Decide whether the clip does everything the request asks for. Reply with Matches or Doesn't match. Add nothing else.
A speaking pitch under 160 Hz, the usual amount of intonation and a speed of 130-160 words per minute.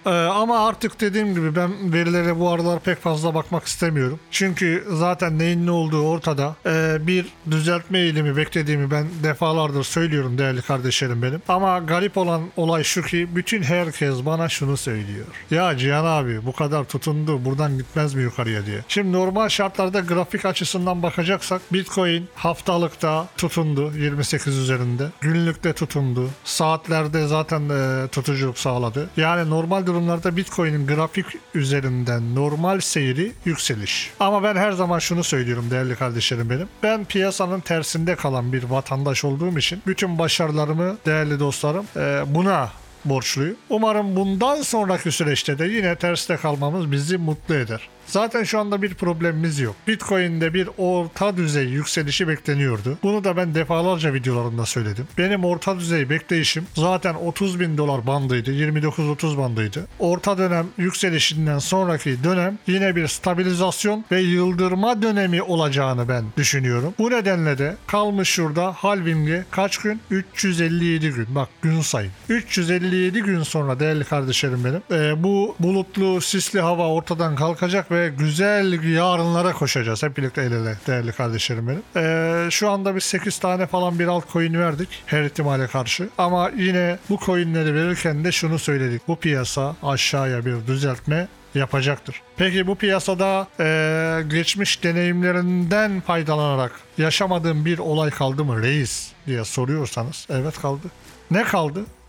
Doesn't match